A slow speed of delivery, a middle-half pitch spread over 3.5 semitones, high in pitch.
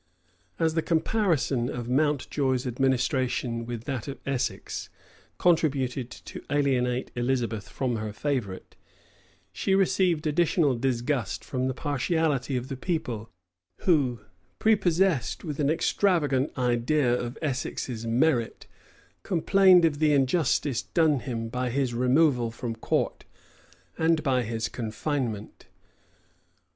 No: slow, 115 wpm; average, 4.3 semitones; low, 130 Hz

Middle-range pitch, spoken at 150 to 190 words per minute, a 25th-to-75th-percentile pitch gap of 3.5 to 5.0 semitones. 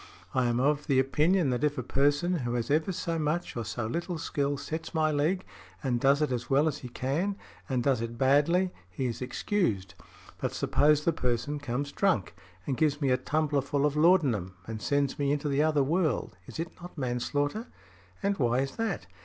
No: medium, 145 Hz; average, 200 wpm; average, 3.8 semitones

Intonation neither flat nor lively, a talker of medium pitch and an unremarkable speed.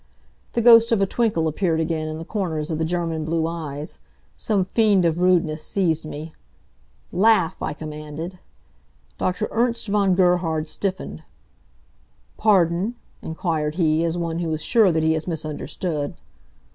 Yes: average, 3.4 semitones; medium, 170 Hz; average, 145 wpm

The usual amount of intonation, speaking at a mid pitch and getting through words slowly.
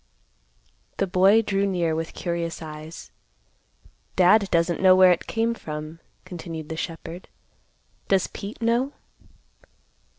Yes: average, 3.3 semitones; medium, 180 Hz; slow, 120 wpm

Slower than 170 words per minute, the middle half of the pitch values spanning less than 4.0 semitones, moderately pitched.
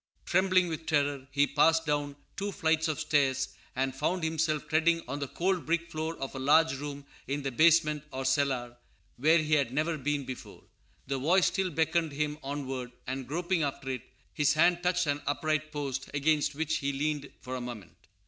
No: average, 185 wpm; average, 2.9 semitones; medium, 150 Hz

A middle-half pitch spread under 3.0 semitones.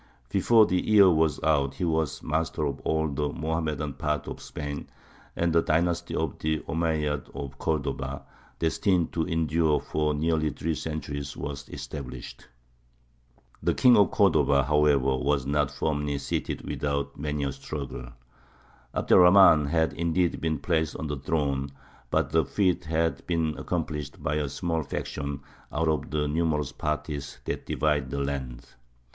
Yes: narrow, 2.4 semitones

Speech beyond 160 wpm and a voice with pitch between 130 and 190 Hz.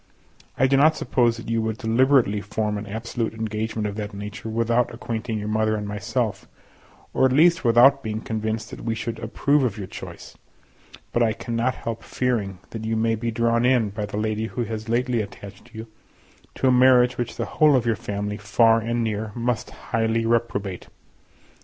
No: average, 190 wpm; low, 115 Hz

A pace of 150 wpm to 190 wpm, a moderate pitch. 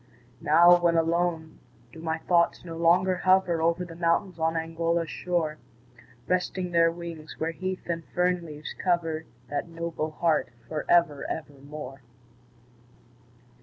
No: slow, 135 wpm; medium, 165 Hz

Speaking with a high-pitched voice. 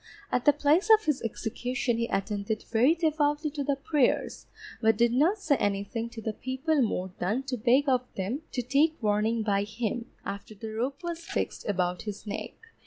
Yes: high, 245 Hz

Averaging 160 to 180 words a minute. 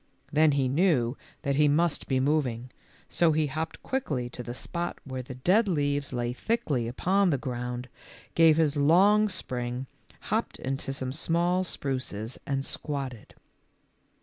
No: average, 150 wpm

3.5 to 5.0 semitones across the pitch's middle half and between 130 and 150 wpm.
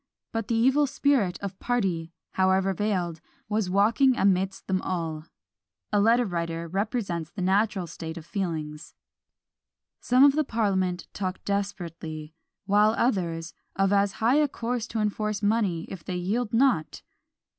Yes: average, 4.3 semitones; average, 145 wpm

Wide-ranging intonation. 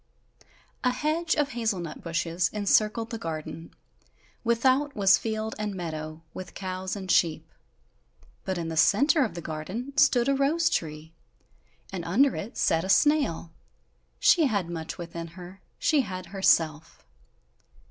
Yes: wide, 7.0 semitones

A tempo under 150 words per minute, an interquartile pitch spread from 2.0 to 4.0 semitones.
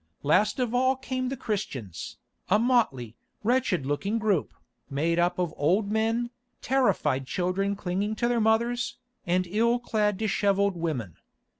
No: average, 140 wpm; average, 5.3 semitones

